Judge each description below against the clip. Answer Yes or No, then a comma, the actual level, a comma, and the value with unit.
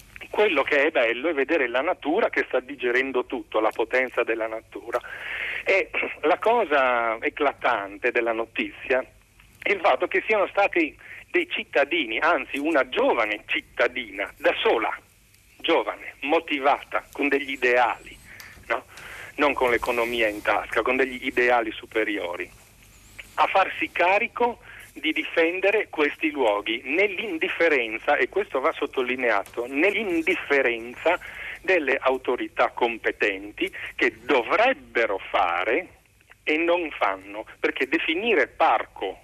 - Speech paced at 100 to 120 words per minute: Yes, slow, 115 wpm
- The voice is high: No, medium, 155 Hz